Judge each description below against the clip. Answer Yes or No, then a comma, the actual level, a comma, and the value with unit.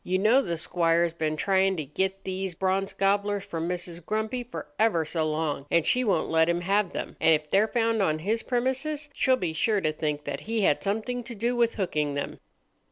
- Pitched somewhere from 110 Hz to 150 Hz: No, high, 190 Hz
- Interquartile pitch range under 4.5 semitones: No, average, 5.2 semitones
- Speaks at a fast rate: Yes, fast, 215 wpm